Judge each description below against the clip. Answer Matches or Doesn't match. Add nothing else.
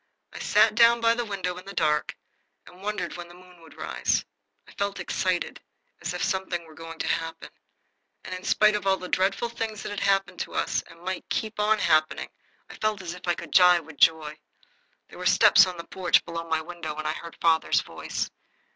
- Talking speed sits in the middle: Doesn't match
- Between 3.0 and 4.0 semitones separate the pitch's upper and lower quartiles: Matches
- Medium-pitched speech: Matches